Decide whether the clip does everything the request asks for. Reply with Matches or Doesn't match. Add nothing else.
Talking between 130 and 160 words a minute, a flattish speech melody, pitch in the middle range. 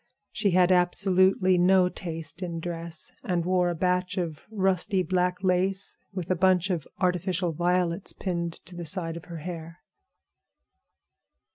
Matches